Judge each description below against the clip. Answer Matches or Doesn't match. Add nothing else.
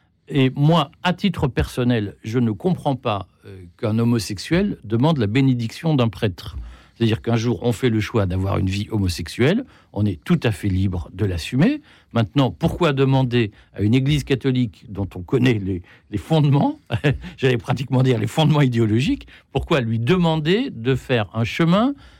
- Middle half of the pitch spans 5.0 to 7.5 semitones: Matches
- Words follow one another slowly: Doesn't match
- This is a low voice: Matches